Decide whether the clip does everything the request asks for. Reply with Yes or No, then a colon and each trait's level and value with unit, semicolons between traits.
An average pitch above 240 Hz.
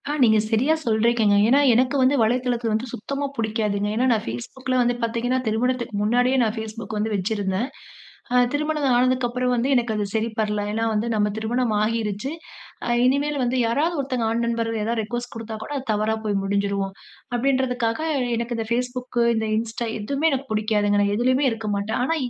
No: high, 230 Hz